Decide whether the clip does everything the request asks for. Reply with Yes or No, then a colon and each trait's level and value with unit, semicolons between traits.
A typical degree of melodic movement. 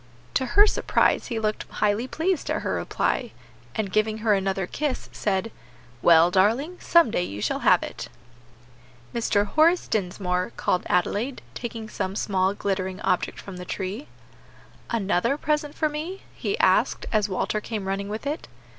No: wide, 5.9 semitones